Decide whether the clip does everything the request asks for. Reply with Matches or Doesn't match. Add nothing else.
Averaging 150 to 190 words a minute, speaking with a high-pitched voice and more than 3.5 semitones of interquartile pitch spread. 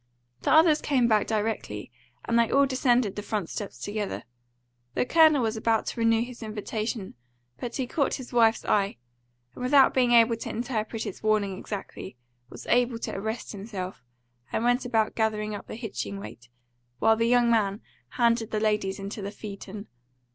Doesn't match